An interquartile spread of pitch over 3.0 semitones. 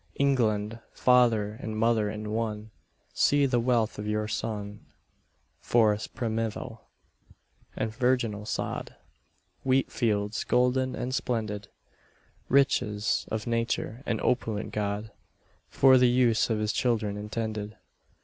No: average, 2.7 semitones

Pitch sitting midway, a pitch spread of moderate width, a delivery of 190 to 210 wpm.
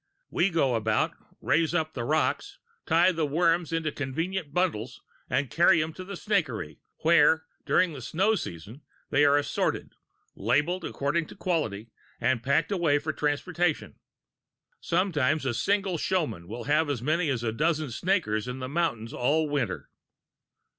No: medium, 155 Hz; average, 5.0 semitones; average, 155 wpm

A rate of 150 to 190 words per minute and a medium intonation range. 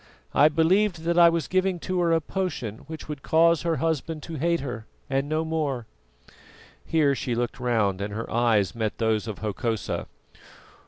No: average, 175 wpm; wide, 6.1 semitones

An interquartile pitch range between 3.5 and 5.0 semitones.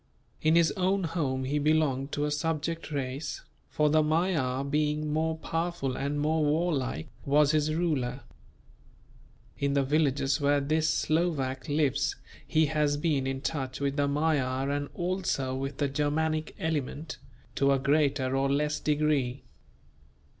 No: narrow, 2.4 semitones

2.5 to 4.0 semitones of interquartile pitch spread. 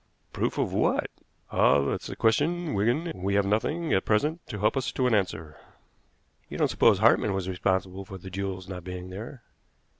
No: average, 4.8 semitones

